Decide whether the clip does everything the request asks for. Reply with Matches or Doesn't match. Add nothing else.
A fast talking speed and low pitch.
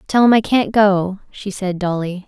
Doesn't match